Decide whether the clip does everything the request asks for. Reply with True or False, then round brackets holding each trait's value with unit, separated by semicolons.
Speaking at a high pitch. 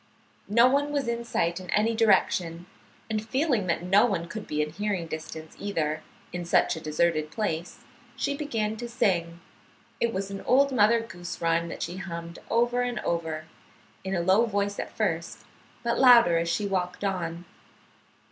True (195 Hz)